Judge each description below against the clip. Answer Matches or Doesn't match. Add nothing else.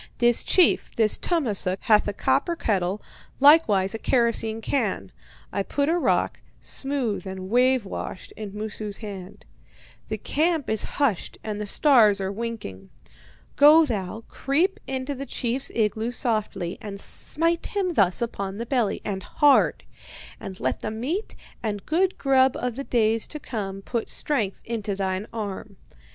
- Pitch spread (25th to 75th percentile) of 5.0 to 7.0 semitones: Matches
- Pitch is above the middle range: Matches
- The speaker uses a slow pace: Doesn't match